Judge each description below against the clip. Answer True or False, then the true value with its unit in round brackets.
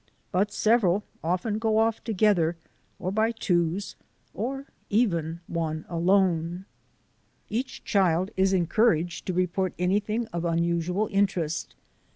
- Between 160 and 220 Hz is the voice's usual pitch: True (185 Hz)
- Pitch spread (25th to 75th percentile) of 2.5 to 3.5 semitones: False (3.9 semitones)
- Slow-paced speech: True (115 wpm)